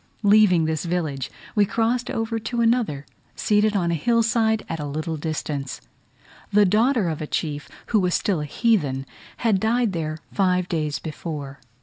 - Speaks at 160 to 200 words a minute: Yes, average, 165 wpm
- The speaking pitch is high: No, medium, 180 Hz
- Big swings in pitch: Yes, wide, 6.2 semitones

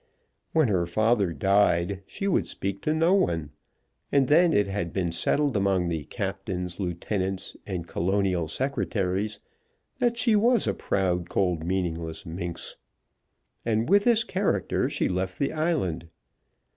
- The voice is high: No, very low, 95 Hz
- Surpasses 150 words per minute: No, average, 140 wpm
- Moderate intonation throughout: No, wide, 8.0 semitones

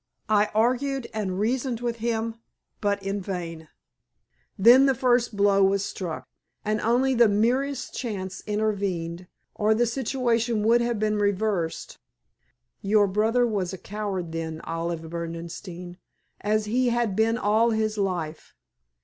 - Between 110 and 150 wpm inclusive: Yes, slow, 135 wpm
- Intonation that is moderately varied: Yes, average, 3.8 semitones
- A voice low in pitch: No, high, 210 Hz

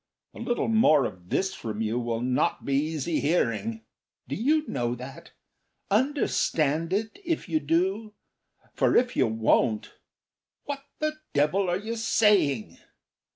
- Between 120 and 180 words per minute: Yes, average, 140 wpm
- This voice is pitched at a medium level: Yes, medium, 160 Hz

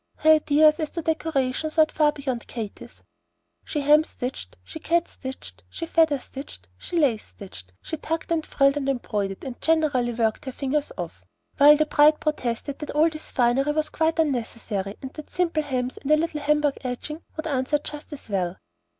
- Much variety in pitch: No, average, 3.7 semitones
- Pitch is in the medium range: No, very high, 290 Hz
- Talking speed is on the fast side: No, average, 185 wpm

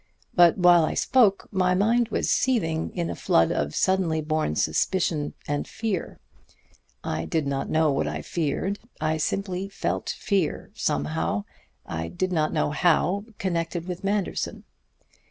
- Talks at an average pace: Yes, average, 145 wpm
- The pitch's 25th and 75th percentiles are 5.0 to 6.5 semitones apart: No, average, 4.2 semitones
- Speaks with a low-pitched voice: No, medium, 170 Hz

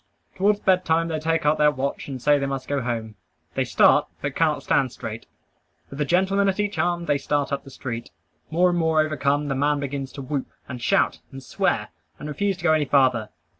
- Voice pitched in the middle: Yes, medium, 145 Hz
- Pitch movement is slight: No, average, 3.5 semitones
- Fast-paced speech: Yes, fast, 220 wpm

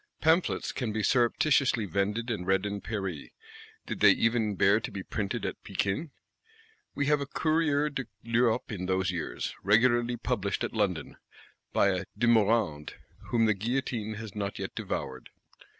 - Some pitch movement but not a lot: Yes, average, 3.7 semitones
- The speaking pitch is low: Yes, low, 110 Hz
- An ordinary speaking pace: Yes, average, 160 wpm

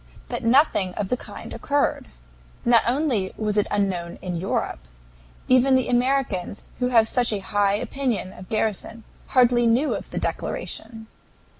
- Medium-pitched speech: No, high, 230 Hz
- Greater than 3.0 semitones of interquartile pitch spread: Yes, average, 4.1 semitones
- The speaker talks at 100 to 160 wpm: Yes, average, 150 wpm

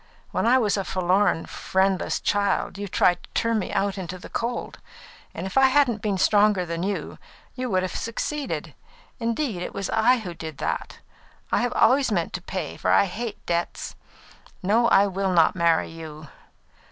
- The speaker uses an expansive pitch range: No, average, 4.2 semitones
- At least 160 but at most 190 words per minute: Yes, average, 175 wpm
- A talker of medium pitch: No, high, 195 Hz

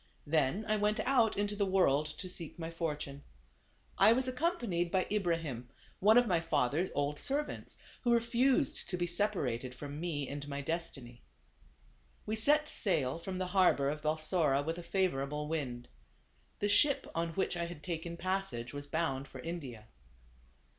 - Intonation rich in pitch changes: Yes, wide, 5.8 semitones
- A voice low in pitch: No, medium, 170 Hz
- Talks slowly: No, average, 165 wpm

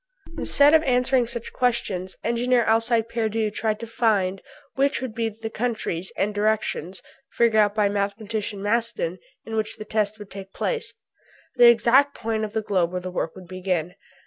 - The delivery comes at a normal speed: Yes, average, 170 wpm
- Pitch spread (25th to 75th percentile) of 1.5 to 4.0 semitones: Yes, average, 2.8 semitones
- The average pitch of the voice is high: Yes, high, 220 Hz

